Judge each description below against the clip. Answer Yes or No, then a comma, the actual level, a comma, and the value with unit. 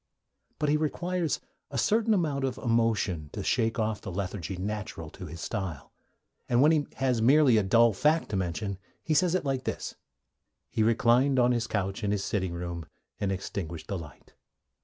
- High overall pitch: No, low, 110 Hz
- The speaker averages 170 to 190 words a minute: Yes, average, 180 wpm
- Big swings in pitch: Yes, wide, 6.2 semitones